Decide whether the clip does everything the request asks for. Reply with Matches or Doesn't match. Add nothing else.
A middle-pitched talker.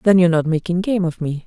Matches